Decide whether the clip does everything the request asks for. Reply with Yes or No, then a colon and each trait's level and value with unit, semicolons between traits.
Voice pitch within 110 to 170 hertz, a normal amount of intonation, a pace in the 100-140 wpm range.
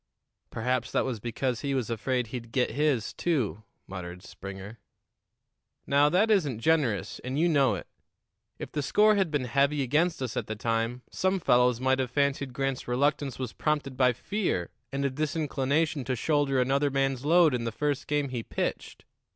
No: low, 135 Hz; average, 3.3 semitones; average, 175 wpm